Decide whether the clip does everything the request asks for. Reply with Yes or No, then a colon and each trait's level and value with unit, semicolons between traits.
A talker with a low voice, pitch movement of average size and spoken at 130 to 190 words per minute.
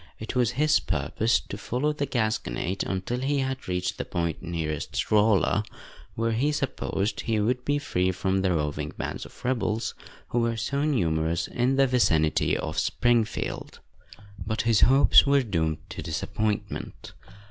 No: low, 110 Hz; wide, 6.0 semitones; average, 155 wpm